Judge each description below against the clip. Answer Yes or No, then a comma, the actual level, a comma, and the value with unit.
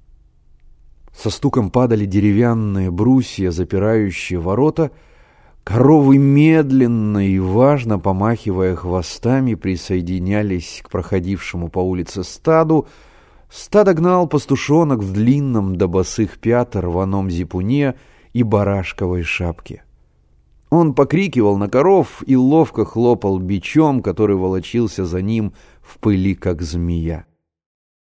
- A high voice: No, low, 100 Hz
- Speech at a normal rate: No, slow, 105 wpm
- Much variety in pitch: Yes, wide, 5.9 semitones